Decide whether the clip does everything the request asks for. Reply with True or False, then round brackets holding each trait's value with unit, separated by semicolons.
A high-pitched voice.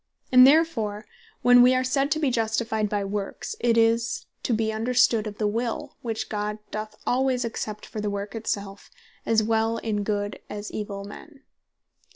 True (220 Hz)